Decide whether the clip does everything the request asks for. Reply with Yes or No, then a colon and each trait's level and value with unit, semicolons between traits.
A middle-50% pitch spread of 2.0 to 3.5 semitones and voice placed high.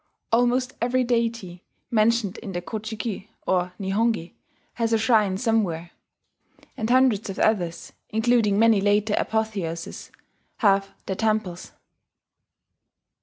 Yes: average, 3.2 semitones; high, 215 Hz